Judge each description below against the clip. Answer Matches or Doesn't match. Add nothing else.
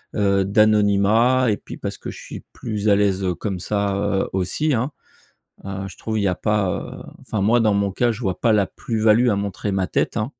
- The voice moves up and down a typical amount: Doesn't match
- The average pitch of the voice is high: Doesn't match